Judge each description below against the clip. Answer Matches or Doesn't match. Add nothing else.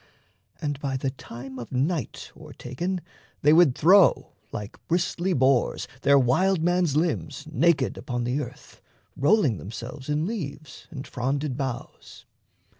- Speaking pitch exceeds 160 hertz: Doesn't match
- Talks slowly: Matches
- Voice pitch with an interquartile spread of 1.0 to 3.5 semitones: Doesn't match